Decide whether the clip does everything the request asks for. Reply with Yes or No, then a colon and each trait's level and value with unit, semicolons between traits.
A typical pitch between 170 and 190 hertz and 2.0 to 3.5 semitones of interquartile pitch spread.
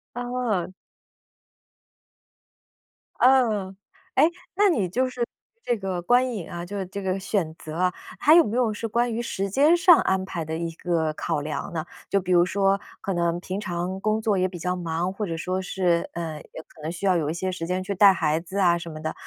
No: medium, 185 Hz; average, 3.9 semitones